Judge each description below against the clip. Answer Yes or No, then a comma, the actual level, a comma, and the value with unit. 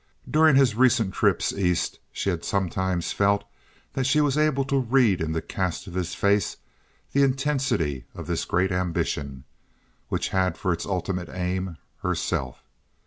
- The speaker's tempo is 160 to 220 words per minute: No, average, 150 wpm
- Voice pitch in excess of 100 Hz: No, very low, 95 Hz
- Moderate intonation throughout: No, wide, 6.7 semitones